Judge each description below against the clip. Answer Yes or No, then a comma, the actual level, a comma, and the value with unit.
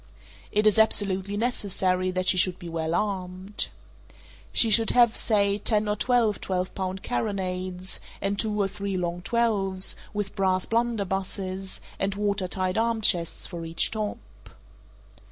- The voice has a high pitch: Yes, high, 195 Hz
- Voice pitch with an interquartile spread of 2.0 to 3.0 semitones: Yes, narrow, 2.4 semitones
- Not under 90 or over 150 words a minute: Yes, average, 145 wpm